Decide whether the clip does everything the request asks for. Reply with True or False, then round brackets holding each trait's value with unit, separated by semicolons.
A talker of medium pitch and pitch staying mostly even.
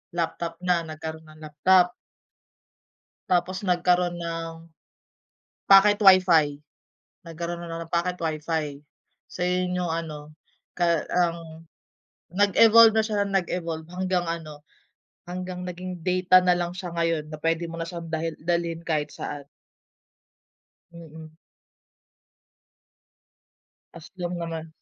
True (170 Hz; 2.0 semitones)